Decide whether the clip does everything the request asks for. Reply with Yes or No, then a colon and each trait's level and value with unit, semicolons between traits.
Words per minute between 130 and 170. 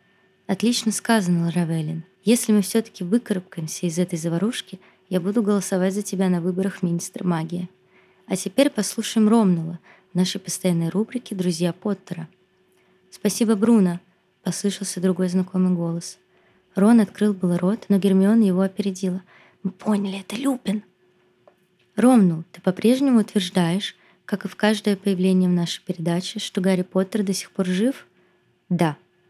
Yes: average, 135 wpm